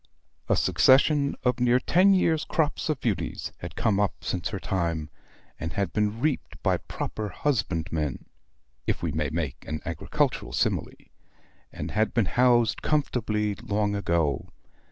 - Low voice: Yes, low, 105 Hz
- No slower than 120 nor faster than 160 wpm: Yes, average, 145 wpm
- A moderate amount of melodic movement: No, wide, 7.0 semitones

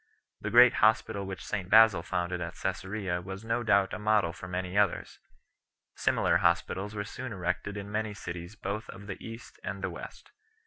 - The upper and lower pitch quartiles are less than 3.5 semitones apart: Yes, average, 2.8 semitones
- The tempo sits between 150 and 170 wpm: No, average, 185 wpm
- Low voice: Yes, low, 100 Hz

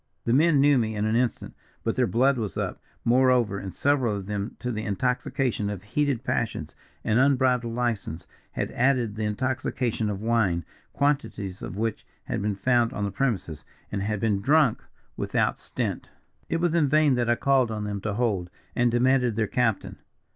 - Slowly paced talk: No, average, 185 wpm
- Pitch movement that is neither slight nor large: Yes, average, 3.9 semitones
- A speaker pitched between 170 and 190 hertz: No, low, 115 Hz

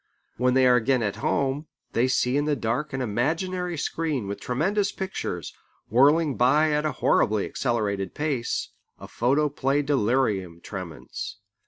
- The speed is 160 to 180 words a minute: No, average, 145 wpm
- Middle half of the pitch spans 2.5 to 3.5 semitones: No, average, 4.3 semitones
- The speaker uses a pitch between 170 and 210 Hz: No, low, 130 Hz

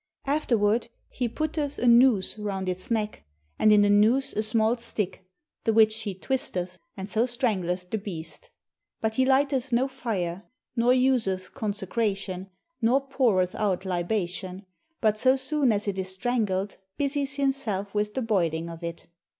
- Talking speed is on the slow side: No, average, 155 wpm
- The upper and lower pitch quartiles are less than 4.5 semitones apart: No, average, 4.8 semitones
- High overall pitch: Yes, high, 215 Hz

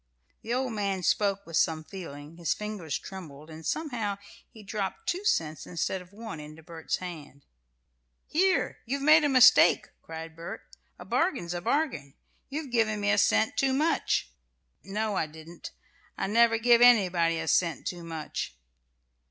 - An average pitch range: No, wide, 6.3 semitones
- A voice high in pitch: Yes, high, 195 Hz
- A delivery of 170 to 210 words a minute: No, average, 160 wpm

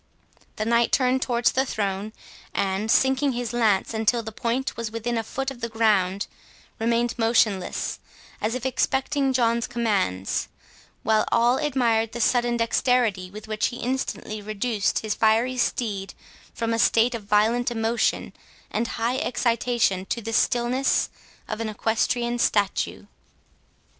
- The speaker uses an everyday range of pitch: No, narrow, 2.1 semitones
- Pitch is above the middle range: Yes, high, 230 Hz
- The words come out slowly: No, average, 145 wpm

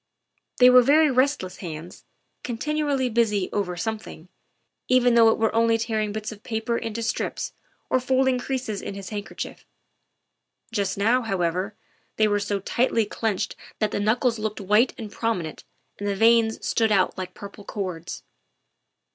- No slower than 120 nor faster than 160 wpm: Yes, average, 155 wpm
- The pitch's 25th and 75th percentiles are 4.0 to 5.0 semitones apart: No, average, 3.0 semitones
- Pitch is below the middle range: No, high, 220 Hz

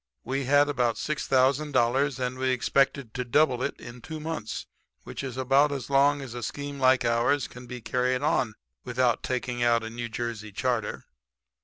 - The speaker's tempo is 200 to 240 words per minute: No, average, 175 wpm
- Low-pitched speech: Yes, low, 130 Hz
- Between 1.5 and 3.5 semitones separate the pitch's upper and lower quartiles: Yes, narrow, 2.5 semitones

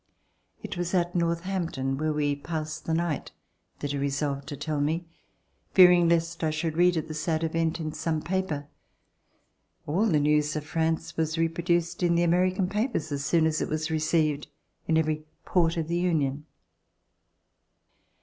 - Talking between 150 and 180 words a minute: Yes, average, 165 wpm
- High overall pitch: No, medium, 160 Hz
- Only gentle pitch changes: Yes, narrow, 2.2 semitones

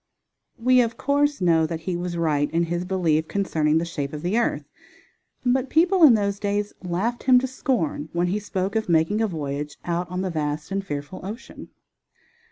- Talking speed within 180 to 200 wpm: Yes, average, 190 wpm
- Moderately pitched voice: Yes, medium, 180 Hz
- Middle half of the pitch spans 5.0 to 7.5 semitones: Yes, wide, 5.5 semitones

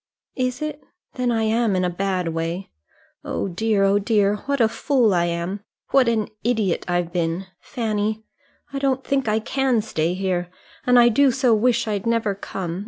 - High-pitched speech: Yes, high, 215 Hz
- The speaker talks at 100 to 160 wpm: No, average, 180 wpm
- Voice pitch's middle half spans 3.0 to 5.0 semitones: Yes, average, 4.5 semitones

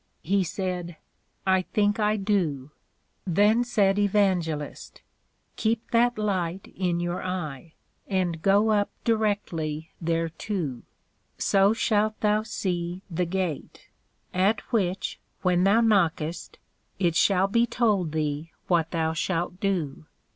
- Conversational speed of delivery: No, slow, 120 wpm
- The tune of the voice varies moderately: Yes, average, 3.7 semitones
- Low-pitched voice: No, medium, 185 Hz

